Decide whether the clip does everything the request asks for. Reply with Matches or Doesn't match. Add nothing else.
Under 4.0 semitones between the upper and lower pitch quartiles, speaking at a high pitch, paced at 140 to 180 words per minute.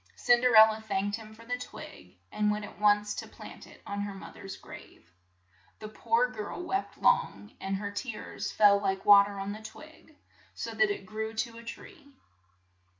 Doesn't match